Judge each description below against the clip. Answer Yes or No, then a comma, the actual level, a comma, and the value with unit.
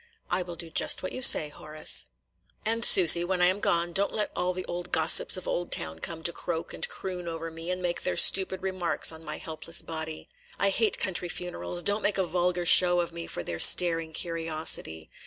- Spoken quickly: Yes, fast, 210 wpm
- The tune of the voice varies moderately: No, narrow, 2.0 semitones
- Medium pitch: Yes, medium, 175 Hz